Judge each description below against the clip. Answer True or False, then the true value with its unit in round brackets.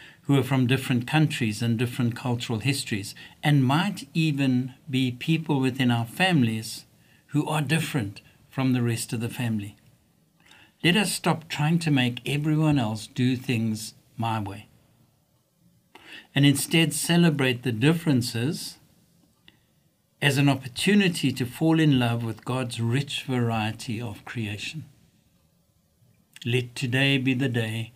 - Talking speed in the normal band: False (130 wpm)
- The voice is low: True (130 Hz)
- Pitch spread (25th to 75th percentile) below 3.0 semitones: False (3.8 semitones)